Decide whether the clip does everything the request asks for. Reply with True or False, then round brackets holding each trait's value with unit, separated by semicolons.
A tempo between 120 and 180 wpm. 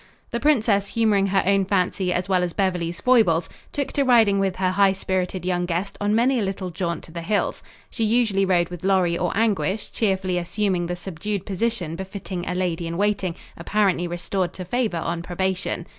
False (190 wpm)